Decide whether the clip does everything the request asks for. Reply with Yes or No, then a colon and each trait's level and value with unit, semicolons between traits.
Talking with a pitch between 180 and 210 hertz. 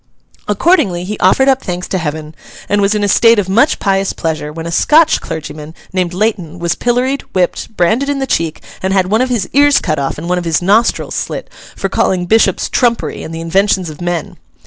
Yes: high, 190 Hz